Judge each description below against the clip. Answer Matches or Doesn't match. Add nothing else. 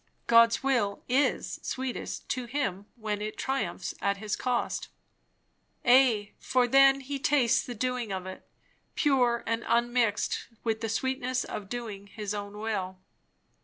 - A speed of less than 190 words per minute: Matches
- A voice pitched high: Matches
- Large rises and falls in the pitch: Doesn't match